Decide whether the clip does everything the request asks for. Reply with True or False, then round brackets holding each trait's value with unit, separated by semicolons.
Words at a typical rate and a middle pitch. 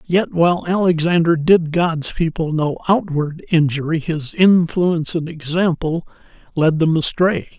False (125 wpm; 165 Hz)